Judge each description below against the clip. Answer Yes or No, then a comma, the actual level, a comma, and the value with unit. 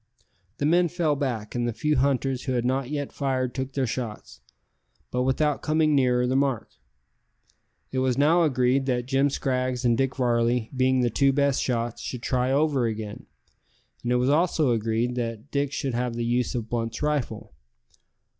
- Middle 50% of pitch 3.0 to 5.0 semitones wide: No, narrow, 2.6 semitones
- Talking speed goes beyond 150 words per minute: Yes, average, 180 wpm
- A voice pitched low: Yes, low, 130 Hz